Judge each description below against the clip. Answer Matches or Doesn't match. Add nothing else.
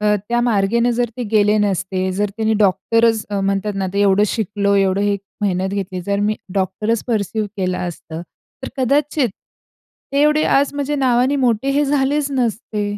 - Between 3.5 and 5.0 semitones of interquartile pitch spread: Matches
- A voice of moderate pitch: Doesn't match